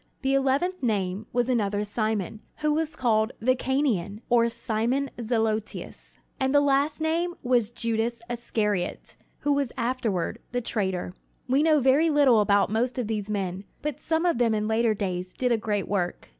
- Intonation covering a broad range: No, average, 4.3 semitones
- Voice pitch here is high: Yes, high, 235 Hz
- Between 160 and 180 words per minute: Yes, average, 170 wpm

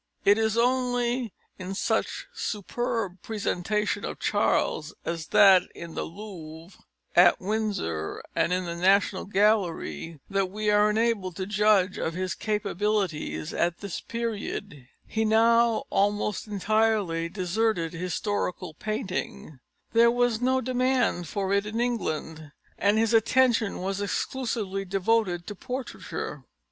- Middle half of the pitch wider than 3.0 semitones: Yes, average, 3.6 semitones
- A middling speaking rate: No, slow, 130 wpm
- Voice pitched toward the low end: No, high, 205 Hz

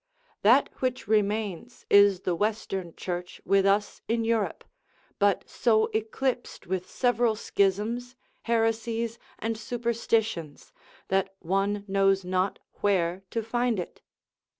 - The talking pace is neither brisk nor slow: No, slow, 115 wpm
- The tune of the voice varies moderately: Yes, average, 3.0 semitones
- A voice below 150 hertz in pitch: No, high, 210 Hz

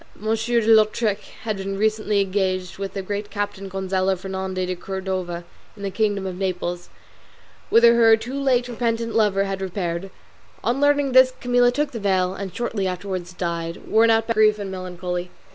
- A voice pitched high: Yes, high, 200 Hz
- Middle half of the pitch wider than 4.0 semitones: No, average, 3.3 semitones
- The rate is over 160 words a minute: Yes, average, 170 wpm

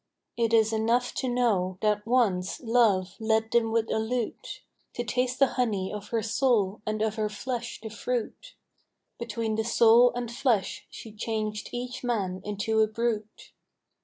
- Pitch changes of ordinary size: No, narrow, 2.3 semitones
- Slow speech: No, average, 160 wpm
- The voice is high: Yes, high, 225 Hz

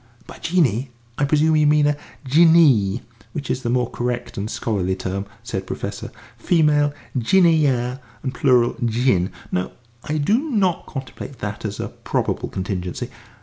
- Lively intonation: Yes, wide, 5.7 semitones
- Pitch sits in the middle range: No, low, 130 Hz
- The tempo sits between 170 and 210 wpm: No, average, 150 wpm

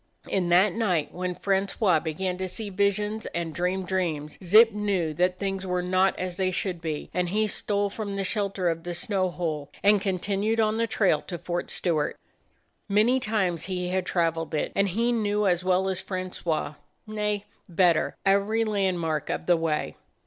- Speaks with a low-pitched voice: No, medium, 185 Hz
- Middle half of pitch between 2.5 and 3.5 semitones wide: Yes, average, 2.8 semitones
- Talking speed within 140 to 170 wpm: No, average, 180 wpm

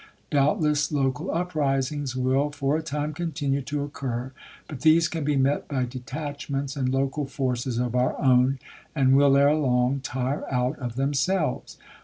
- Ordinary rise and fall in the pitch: No, narrow, 2.2 semitones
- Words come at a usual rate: Yes, average, 160 wpm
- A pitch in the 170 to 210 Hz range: No, medium, 140 Hz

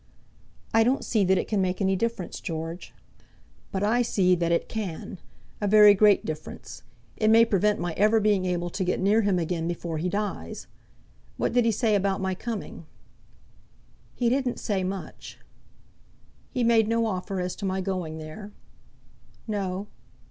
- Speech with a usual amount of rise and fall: Yes, average, 3.1 semitones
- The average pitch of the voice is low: No, high, 195 Hz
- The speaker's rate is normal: Yes, average, 165 wpm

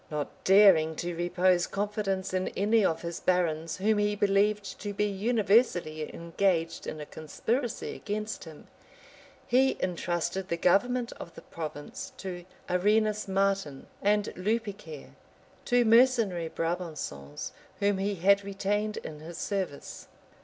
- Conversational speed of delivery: No, slow, 130 wpm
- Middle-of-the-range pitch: No, high, 195 Hz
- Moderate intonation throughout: Yes, average, 3.6 semitones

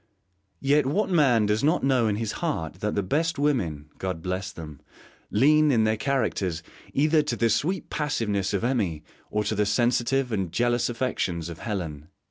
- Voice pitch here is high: No, low, 110 Hz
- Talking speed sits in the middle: Yes, average, 175 wpm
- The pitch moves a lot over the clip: Yes, wide, 6.6 semitones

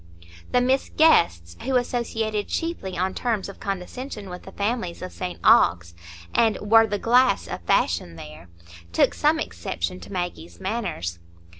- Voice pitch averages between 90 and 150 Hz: No, high, 195 Hz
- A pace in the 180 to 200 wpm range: No, average, 150 wpm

